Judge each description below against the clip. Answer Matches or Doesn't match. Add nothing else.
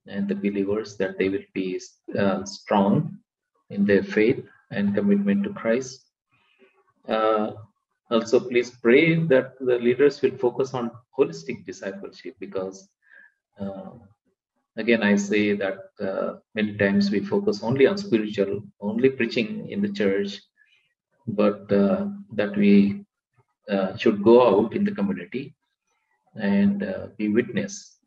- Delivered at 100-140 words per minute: Matches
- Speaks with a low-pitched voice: Matches